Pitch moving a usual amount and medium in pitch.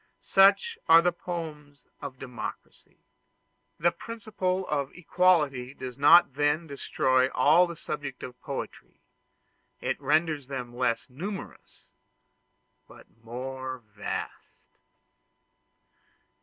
Yes: average, 4.9 semitones; medium, 145 Hz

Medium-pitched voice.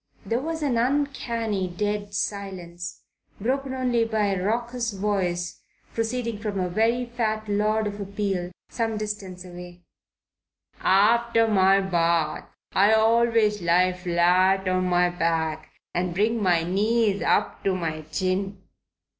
No: high, 200 Hz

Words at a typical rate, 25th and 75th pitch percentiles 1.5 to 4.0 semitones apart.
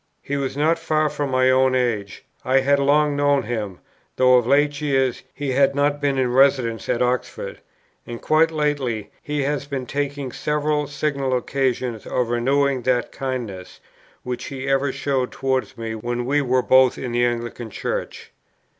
Yes: average, 170 wpm; narrow, 2.6 semitones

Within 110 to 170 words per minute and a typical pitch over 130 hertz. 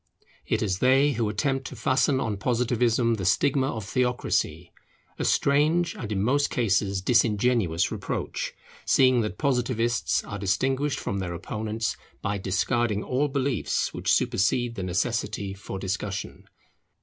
No: slow, 135 wpm; low, 115 Hz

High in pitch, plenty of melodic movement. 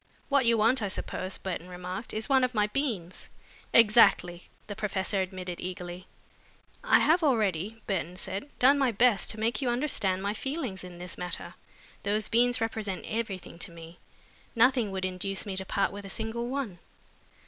No: high, 205 Hz; average, 4.3 semitones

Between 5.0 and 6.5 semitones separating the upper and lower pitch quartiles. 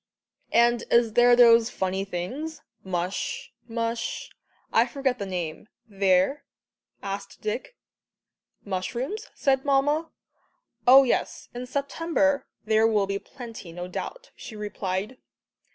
Yes: wide, 5.4 semitones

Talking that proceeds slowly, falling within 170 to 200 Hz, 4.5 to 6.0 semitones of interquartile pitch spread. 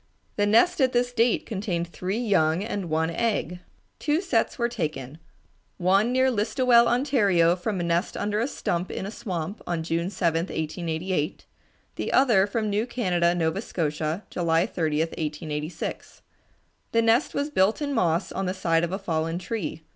No: average, 165 wpm; medium, 185 Hz; wide, 5.5 semitones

